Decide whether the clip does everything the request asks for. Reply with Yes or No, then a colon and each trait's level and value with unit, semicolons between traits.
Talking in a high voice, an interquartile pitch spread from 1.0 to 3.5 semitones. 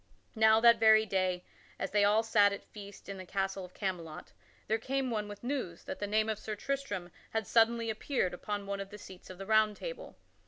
Yes: high, 210 Hz; narrow, 2.4 semitones